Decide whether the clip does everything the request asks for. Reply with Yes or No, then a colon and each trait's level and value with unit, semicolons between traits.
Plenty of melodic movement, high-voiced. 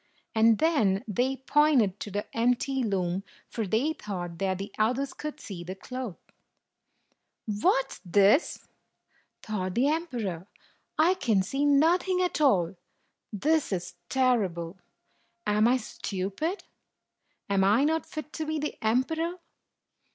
Yes: wide, 6.9 semitones; high, 230 Hz